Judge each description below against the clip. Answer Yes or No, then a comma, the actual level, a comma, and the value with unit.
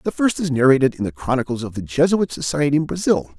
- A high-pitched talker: No, medium, 145 Hz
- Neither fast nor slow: No, fast, 230 wpm